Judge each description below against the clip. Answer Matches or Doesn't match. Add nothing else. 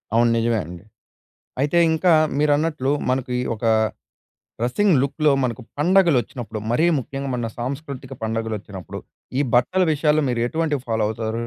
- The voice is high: Doesn't match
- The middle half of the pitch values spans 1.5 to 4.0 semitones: Doesn't match